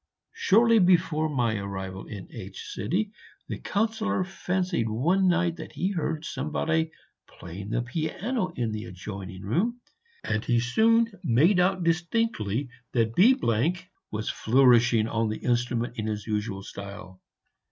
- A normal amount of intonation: No, wide, 9.0 semitones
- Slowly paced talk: Yes, slow, 130 wpm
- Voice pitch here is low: Yes, low, 125 Hz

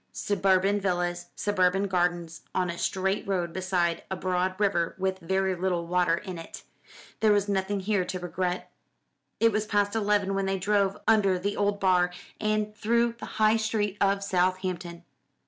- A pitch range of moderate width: No, narrow, 2.2 semitones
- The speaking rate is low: No, average, 165 wpm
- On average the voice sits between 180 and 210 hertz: Yes, high, 190 Hz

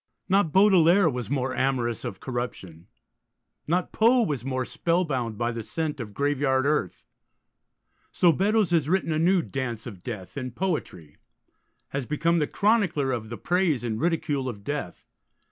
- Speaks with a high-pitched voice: No, medium, 140 Hz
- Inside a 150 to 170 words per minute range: Yes, average, 155 wpm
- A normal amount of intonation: No, wide, 6.1 semitones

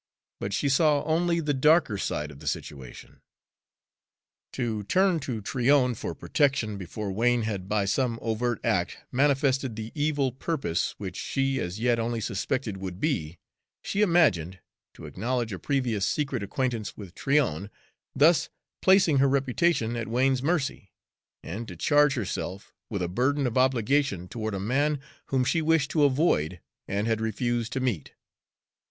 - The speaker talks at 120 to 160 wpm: Yes, average, 155 wpm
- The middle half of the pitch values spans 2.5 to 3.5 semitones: No, average, 5.3 semitones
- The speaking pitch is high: No, low, 125 Hz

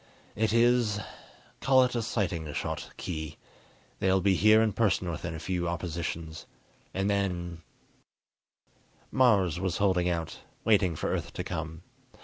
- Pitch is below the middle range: Yes, very low, 95 Hz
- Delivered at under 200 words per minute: Yes, average, 140 wpm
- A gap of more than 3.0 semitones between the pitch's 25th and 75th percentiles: Yes, average, 4.0 semitones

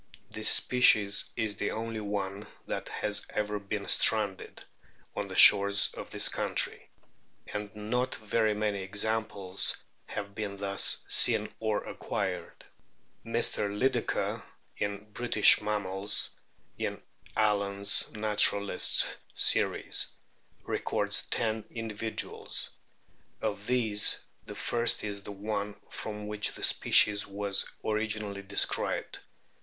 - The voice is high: No, low, 105 Hz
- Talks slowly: Yes, slow, 110 wpm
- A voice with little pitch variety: Yes, narrow, 1.2 semitones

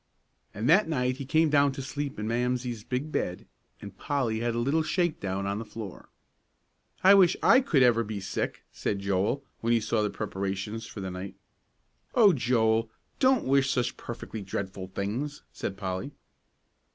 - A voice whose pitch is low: Yes, low, 115 Hz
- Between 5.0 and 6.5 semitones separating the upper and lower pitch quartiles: Yes, wide, 5.6 semitones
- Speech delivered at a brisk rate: No, average, 175 wpm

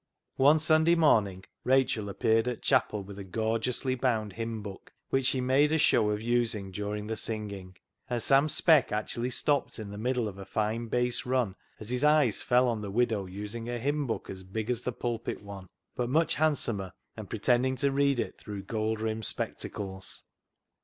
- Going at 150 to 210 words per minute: Yes, average, 190 wpm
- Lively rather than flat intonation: No, average, 3.7 semitones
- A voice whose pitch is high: No, low, 115 Hz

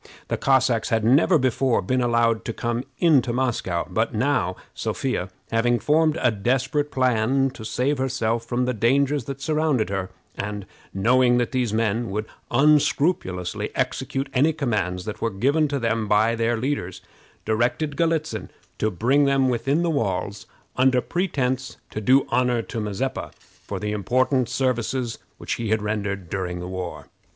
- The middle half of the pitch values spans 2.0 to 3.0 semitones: No, average, 3.8 semitones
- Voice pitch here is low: Yes, low, 120 Hz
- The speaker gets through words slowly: No, average, 160 wpm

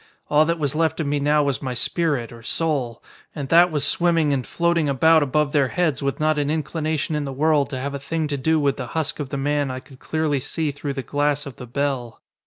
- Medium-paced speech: No, fast, 245 wpm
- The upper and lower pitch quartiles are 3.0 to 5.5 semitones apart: No, narrow, 2.4 semitones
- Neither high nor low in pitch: Yes, medium, 145 Hz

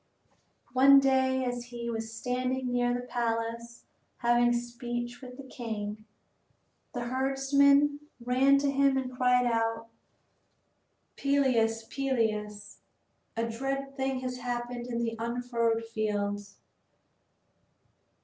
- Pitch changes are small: Yes, narrow, 2.3 semitones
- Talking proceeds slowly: Yes, slow, 110 wpm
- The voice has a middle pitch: No, high, 245 Hz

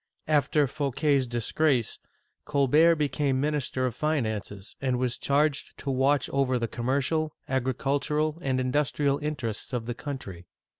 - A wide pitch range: No, average, 3.0 semitones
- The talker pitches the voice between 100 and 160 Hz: Yes, low, 135 Hz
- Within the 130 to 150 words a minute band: Yes, slow, 135 wpm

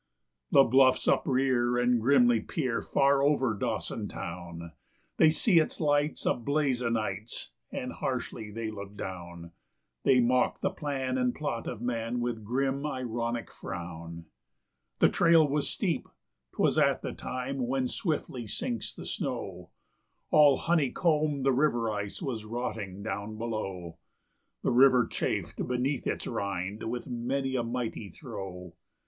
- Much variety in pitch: No, average, 4.2 semitones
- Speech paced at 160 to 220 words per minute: No, average, 140 wpm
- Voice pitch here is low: Yes, low, 125 Hz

